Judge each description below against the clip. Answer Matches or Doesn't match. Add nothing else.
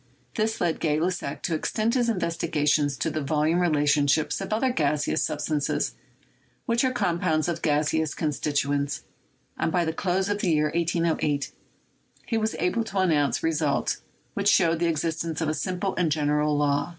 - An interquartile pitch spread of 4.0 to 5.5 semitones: Doesn't match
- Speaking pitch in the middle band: Matches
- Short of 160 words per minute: Doesn't match